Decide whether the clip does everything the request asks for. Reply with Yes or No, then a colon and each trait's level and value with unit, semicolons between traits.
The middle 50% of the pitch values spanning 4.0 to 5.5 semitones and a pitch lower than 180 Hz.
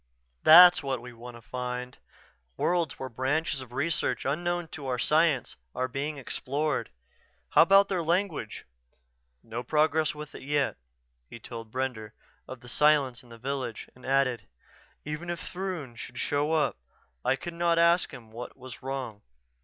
Yes: average, 4.4 semitones; low, 135 Hz